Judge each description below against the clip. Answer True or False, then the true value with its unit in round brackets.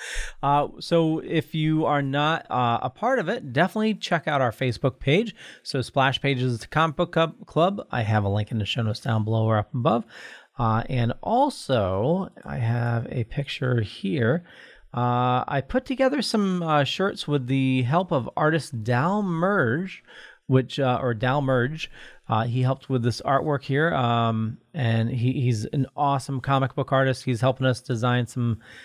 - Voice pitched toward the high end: False (135 Hz)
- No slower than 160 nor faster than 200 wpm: True (175 wpm)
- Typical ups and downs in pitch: True (4.7 semitones)